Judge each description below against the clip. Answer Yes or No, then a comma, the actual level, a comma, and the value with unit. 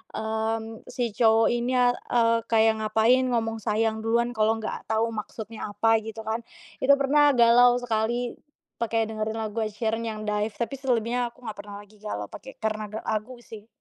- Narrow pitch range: Yes, narrow, 1.6 semitones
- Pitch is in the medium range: No, high, 225 Hz